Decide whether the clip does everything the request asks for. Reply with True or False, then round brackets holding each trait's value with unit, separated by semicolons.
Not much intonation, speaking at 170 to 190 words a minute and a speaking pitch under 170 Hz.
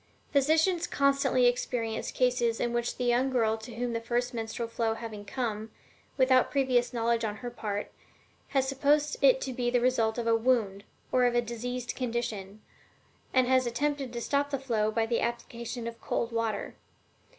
False (2.1 semitones; 175 wpm; 240 Hz)